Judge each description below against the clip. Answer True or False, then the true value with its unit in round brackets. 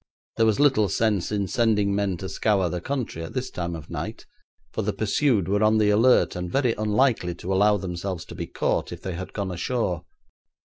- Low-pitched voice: True (100 Hz)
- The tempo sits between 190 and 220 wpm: True (205 wpm)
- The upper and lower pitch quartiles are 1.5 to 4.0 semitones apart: True (3.6 semitones)